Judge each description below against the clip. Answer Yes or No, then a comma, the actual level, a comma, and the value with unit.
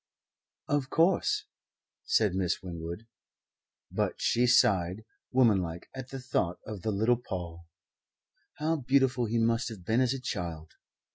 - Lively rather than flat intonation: Yes, wide, 6.1 semitones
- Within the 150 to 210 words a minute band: No, slow, 135 wpm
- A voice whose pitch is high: No, low, 110 Hz